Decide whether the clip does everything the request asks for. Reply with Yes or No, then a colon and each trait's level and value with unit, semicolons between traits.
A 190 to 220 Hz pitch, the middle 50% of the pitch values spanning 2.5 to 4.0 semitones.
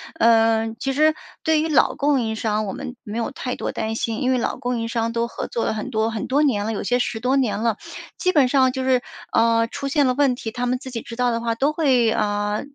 No: high, 240 Hz; average, 2.9 semitones